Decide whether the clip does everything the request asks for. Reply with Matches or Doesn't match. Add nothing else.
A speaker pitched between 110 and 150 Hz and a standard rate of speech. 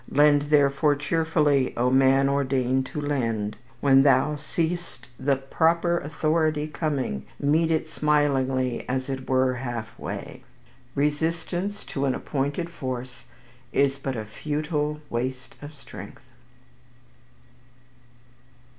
Doesn't match